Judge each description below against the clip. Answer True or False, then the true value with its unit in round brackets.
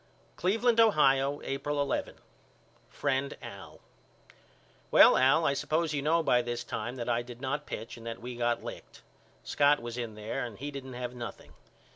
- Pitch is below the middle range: True (130 Hz)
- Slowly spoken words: False (170 wpm)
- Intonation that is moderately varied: True (3.4 semitones)